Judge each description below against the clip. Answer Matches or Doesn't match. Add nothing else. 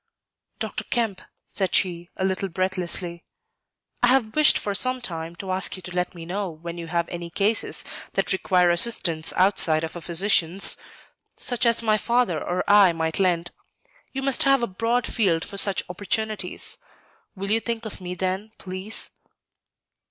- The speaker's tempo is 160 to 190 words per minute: Matches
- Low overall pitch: Doesn't match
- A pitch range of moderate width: Matches